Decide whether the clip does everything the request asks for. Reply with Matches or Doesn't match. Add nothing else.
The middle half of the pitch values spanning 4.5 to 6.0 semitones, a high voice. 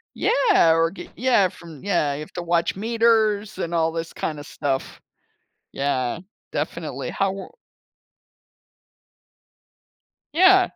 Doesn't match